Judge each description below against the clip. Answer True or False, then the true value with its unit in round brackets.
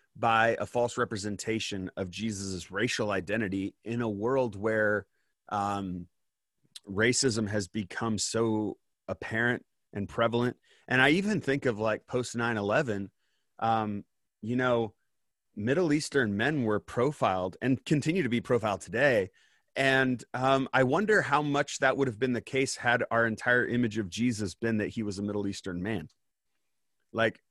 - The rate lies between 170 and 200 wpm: False (155 wpm)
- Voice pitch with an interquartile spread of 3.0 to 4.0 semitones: True (3.5 semitones)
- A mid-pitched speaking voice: False (115 Hz)